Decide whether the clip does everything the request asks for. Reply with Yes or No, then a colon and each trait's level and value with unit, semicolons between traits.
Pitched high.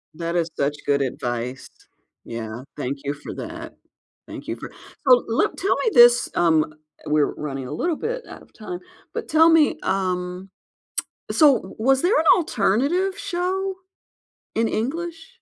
Yes: high, 220 Hz